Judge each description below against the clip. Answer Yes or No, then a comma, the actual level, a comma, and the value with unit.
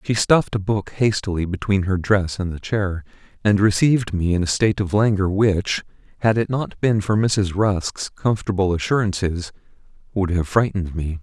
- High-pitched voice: No, low, 100 Hz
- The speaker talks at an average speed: Yes, average, 175 wpm